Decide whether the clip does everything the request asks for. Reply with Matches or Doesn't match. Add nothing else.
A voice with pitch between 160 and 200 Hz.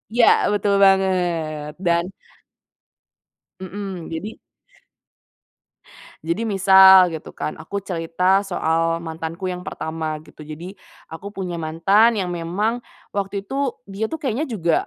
Matches